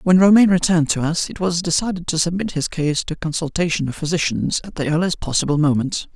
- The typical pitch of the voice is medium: Yes, medium, 165 Hz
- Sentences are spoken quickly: Yes, fast, 215 wpm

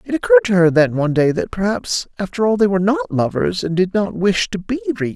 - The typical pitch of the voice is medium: No, high, 195 Hz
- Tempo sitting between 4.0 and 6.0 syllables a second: No, 6.5 syllables/s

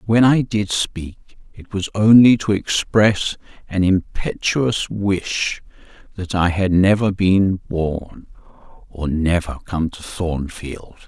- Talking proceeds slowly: Yes, slow, 125 wpm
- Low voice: Yes, very low, 95 Hz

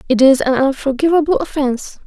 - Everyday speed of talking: Yes, average, 145 wpm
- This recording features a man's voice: No, female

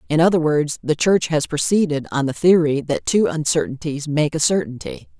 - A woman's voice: Yes, female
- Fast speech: No, average, 185 wpm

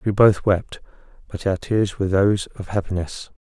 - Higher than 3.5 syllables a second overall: Yes, 5.2 syllables/s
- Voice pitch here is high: No, low, 100 Hz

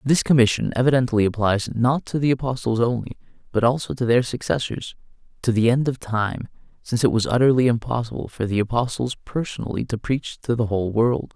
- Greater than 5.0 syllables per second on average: Yes, 5.7 syllables/s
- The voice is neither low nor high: No, low, 120 Hz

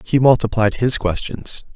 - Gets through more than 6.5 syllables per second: No, 4.4 syllables/s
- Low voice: Yes, low, 115 Hz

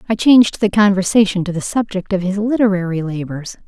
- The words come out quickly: No, average, 180 wpm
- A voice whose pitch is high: Yes, high, 195 Hz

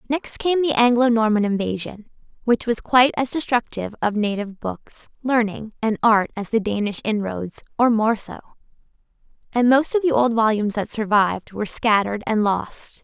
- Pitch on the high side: Yes, high, 225 Hz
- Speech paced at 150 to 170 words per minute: Yes, average, 165 wpm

